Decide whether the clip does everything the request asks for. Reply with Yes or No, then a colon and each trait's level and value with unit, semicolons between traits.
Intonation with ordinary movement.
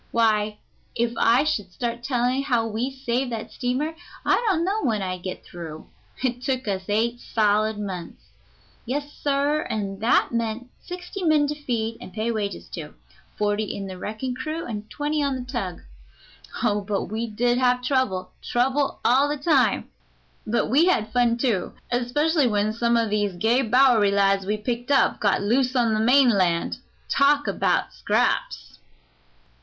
Yes: average, 4.2 semitones